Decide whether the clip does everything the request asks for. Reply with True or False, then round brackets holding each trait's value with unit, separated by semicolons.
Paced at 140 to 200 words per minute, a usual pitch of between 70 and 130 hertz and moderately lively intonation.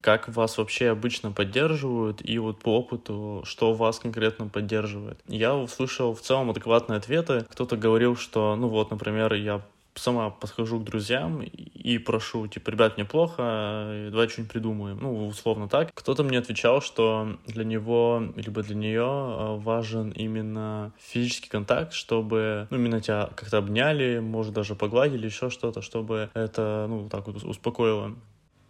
False (150 wpm; 110 Hz; 1.7 semitones)